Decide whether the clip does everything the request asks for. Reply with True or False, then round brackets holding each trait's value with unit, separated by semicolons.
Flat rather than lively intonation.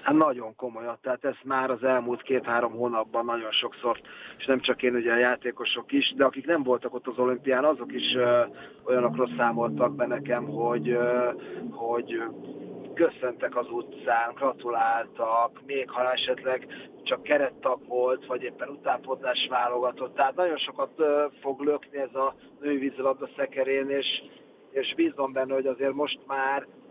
True (2.0 semitones)